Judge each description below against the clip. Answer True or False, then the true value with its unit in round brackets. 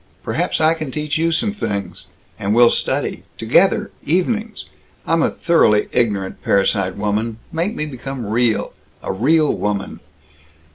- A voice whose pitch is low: True (125 Hz)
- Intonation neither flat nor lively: False (7.7 semitones)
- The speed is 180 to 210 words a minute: False (140 wpm)